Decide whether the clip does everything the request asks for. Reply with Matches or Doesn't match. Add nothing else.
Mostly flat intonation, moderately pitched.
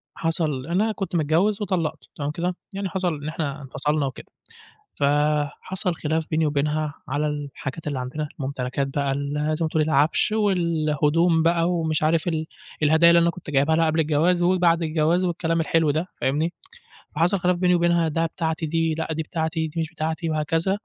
Matches